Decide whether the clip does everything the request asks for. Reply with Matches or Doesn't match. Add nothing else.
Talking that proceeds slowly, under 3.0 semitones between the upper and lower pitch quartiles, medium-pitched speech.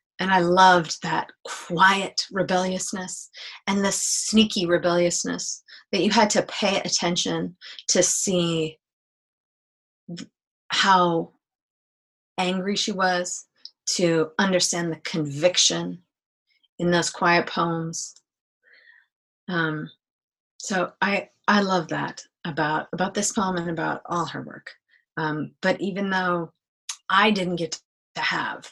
Matches